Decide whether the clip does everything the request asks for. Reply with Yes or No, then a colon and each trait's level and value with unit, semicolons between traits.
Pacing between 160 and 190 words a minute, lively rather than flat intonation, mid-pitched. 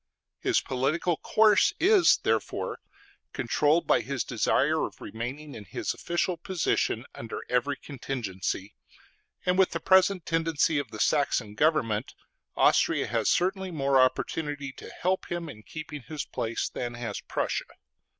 No: average, 140 wpm; wide, 5.9 semitones; medium, 145 Hz